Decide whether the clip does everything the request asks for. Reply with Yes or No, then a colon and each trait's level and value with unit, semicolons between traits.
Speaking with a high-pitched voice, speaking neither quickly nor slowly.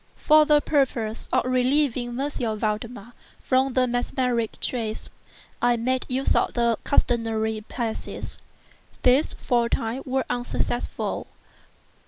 No: high, 245 Hz; slow, 120 wpm